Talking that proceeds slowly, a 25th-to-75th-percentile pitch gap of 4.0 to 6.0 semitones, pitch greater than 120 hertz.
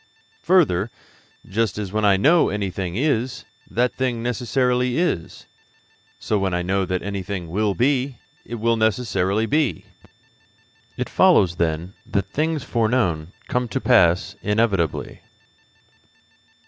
No: slow, 125 wpm; average, 4.8 semitones; low, 110 Hz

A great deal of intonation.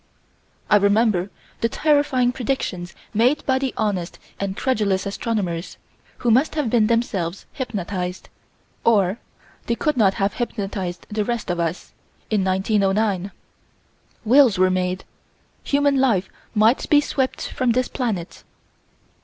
No: average, 4.8 semitones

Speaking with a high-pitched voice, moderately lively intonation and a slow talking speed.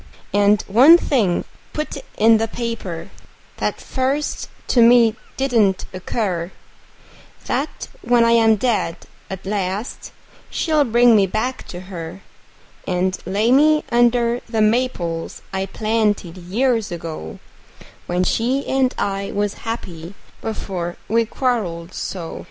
Yes: high, 215 Hz; average, 4.4 semitones; slow, 125 wpm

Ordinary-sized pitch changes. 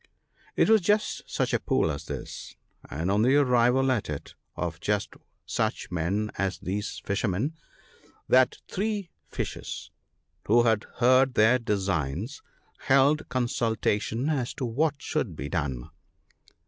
No: wide, 5.7 semitones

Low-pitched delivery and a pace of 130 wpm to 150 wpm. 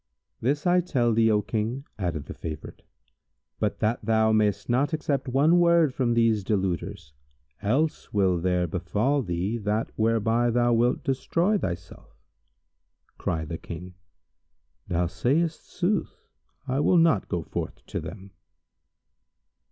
Yes: low, 115 Hz; slow, 135 wpm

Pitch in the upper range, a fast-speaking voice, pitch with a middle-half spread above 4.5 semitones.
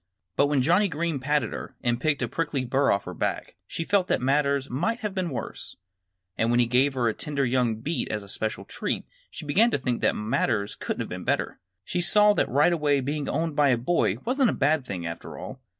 No: medium, 140 Hz; fast, 230 wpm; average, 5.0 semitones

